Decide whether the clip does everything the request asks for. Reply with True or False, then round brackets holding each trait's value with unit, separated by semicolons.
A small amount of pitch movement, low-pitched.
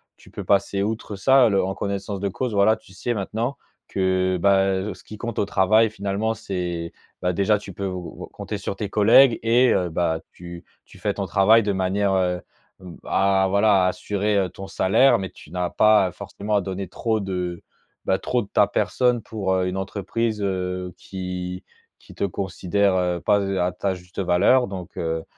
True (2.2 semitones; 95 Hz)